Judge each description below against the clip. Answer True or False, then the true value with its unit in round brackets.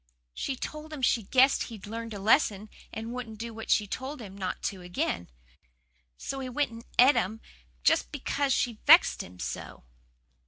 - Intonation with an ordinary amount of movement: True (4.3 semitones)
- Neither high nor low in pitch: False (230 Hz)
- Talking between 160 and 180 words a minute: True (170 wpm)